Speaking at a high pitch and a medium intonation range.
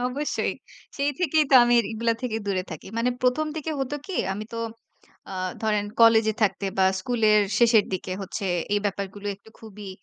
Yes: high, 220 Hz; average, 3.7 semitones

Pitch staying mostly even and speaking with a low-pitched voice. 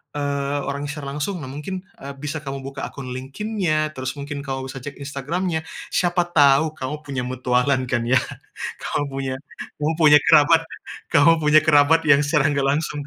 No: narrow, 2.3 semitones; medium, 145 Hz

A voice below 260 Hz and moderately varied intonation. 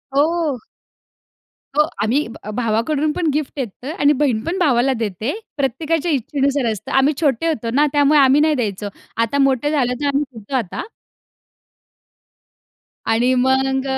No: very high, 270 Hz; average, 3.8 semitones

